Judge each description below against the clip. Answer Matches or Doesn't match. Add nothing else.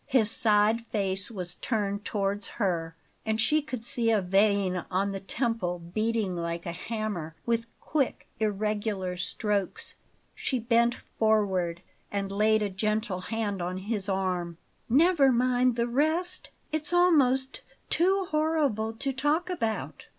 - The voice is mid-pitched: Doesn't match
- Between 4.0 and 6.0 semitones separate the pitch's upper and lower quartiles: Matches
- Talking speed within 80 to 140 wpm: Matches